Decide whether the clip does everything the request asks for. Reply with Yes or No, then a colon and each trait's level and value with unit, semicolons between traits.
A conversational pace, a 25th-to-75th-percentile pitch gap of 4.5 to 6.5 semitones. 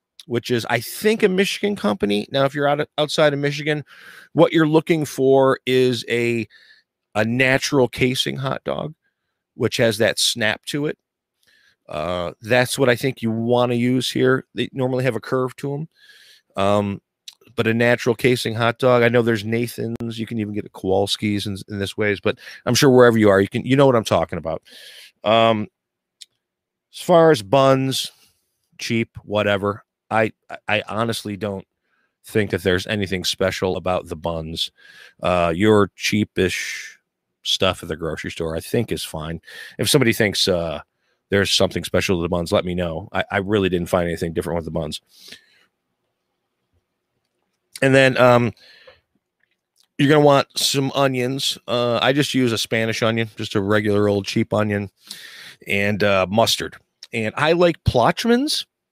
Yes: average, 170 wpm; average, 4.9 semitones